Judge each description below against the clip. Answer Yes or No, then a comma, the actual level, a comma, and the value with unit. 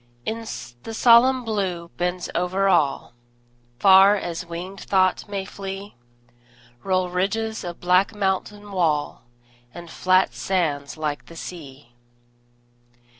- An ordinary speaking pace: No, slow, 110 wpm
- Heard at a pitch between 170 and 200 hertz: Yes, medium, 185 Hz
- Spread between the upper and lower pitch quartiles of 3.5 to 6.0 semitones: No, average, 2.9 semitones